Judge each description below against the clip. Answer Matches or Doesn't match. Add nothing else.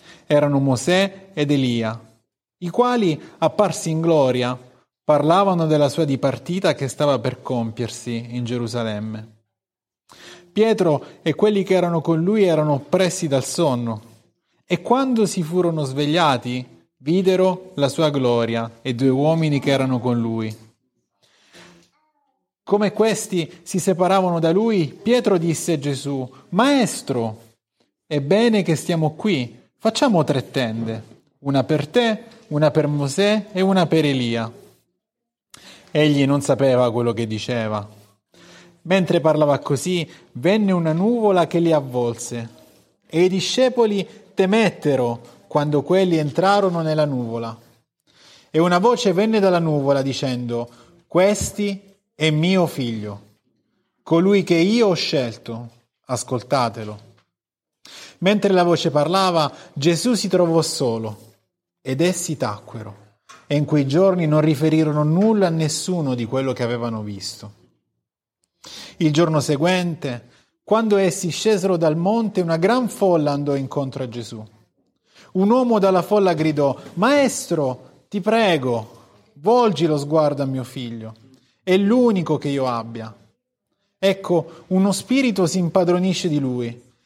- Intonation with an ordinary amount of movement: Doesn't match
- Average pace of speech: Matches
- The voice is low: Doesn't match